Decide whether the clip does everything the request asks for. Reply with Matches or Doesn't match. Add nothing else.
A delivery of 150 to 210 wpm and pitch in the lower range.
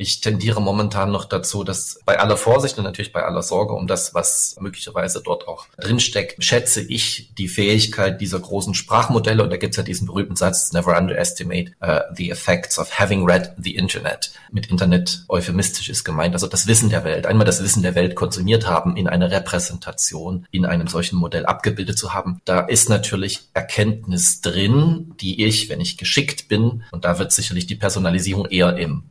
Matches